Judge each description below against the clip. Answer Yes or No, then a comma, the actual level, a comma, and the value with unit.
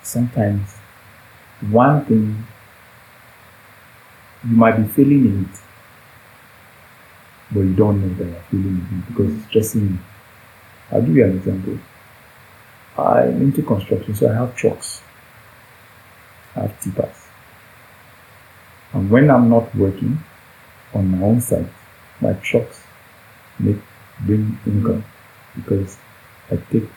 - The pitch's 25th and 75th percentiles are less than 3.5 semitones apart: Yes, average, 3.1 semitones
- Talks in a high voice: No, low, 110 Hz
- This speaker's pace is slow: Yes, slow, 120 wpm